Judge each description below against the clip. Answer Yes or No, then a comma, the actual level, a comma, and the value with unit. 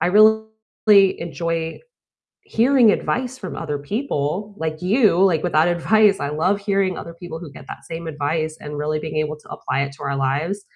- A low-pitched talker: No, medium, 170 Hz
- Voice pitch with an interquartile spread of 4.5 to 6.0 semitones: Yes, average, 4.9 semitones